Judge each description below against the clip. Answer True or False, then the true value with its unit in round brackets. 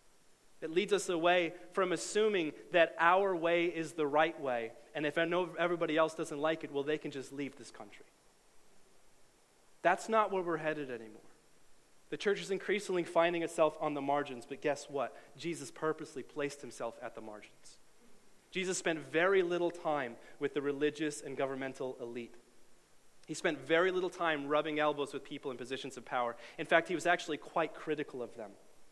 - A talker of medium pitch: True (155 Hz)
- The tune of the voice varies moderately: True (3.5 semitones)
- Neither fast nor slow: True (180 wpm)